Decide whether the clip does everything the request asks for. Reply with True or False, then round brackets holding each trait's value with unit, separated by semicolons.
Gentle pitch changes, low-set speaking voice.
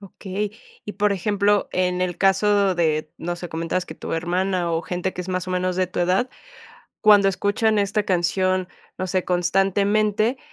False (2.3 semitones; 185 Hz)